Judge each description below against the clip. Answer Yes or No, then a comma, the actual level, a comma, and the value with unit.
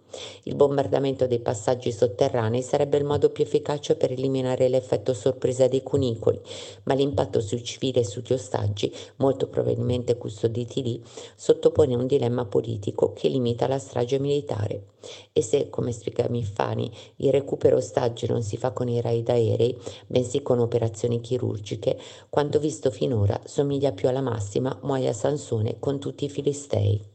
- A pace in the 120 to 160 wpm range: Yes, average, 150 wpm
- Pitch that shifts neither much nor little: Yes, average, 3.1 semitones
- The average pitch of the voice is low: Yes, low, 130 Hz